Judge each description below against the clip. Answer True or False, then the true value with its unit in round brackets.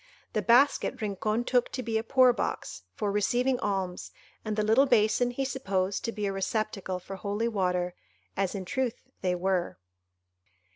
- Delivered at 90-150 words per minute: False (165 wpm)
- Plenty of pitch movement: False (4.1 semitones)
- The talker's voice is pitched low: False (215 Hz)